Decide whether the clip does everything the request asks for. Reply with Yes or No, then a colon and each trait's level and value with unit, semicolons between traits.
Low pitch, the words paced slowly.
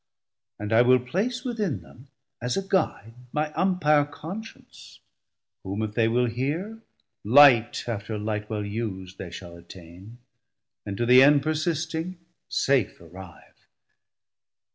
Yes: low, 125 Hz; slow, 130 wpm